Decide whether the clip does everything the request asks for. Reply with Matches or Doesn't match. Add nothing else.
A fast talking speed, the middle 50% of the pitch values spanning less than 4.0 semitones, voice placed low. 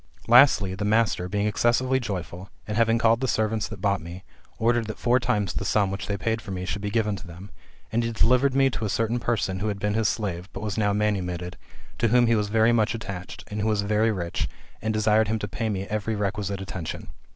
Matches